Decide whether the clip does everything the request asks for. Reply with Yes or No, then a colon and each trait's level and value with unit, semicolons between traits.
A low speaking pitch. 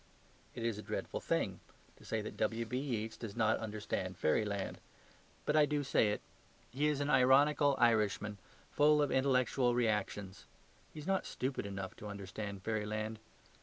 Yes: low, 115 Hz